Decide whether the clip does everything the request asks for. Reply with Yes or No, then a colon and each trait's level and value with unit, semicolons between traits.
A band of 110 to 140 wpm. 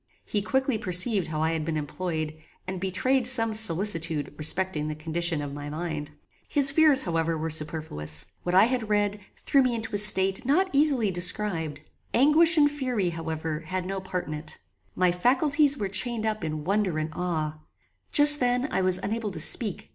No: average, 180 wpm